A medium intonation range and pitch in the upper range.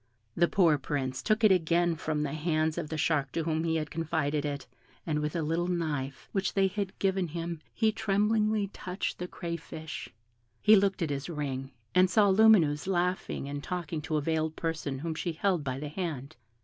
No: average, 3.5 semitones; medium, 165 Hz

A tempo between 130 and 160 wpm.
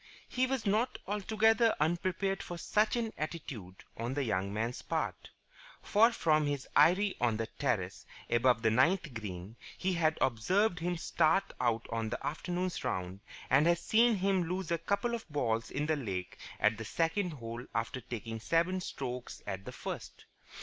No: average, 170 wpm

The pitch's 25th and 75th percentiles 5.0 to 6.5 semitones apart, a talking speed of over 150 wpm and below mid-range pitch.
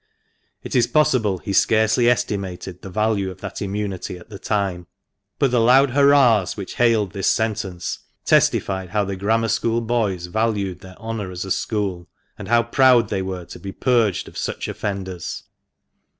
No: average, 3.5 semitones; average, 165 wpm; low, 105 Hz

